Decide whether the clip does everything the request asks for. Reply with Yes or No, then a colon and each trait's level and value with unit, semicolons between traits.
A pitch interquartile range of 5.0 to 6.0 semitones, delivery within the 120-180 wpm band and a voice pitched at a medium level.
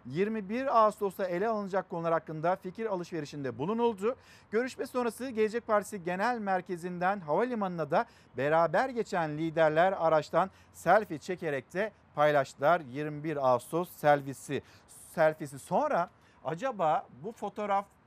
No: average, 5.3 semitones; average, 110 wpm; medium, 180 Hz